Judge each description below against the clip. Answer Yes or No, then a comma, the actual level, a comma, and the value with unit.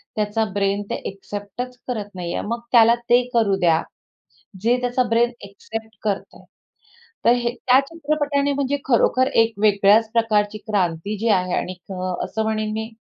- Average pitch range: Yes, average, 3.2 semitones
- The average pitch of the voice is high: Yes, high, 220 Hz